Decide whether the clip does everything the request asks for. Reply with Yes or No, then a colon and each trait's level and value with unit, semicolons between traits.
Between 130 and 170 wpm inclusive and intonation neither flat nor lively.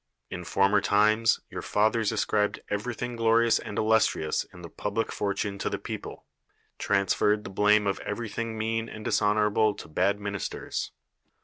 No: average, 150 wpm; narrow, 1.8 semitones